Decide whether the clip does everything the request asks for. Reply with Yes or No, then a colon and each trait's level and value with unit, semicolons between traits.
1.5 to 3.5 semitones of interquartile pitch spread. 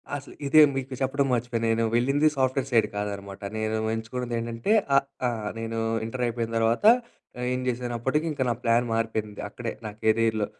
Yes: narrow, 2.4 semitones